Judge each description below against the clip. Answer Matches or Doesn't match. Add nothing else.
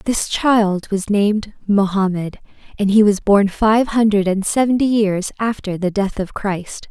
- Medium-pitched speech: Doesn't match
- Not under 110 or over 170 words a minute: Matches